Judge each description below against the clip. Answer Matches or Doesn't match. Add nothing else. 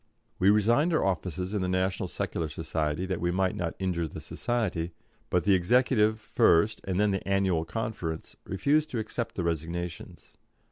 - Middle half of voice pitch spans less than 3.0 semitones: Doesn't match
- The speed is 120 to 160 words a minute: Doesn't match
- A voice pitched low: Matches